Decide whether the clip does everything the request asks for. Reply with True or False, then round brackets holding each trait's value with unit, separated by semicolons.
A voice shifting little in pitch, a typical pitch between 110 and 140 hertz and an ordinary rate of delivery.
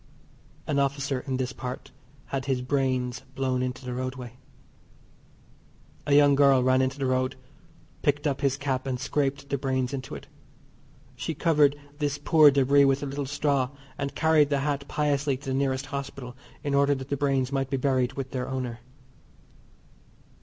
True (1.6 semitones; 135 Hz; 170 wpm)